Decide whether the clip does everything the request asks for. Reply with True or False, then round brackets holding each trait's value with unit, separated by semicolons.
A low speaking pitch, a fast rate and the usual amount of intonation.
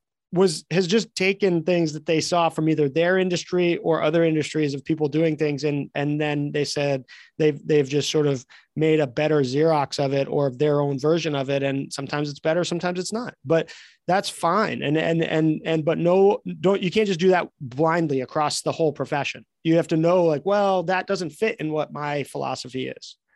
False (160 Hz; 210 wpm; 3.2 semitones)